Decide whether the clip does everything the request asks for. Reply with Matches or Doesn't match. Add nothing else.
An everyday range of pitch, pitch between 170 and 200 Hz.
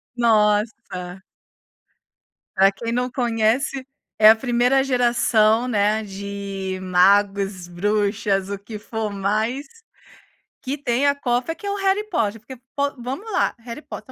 Doesn't match